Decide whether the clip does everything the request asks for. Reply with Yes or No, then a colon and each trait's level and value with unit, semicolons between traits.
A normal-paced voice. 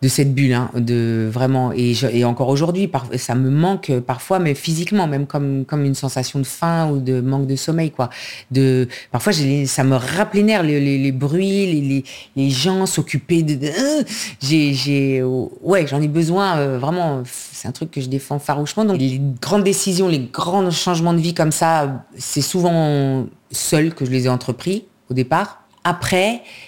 Yes: average, 185 wpm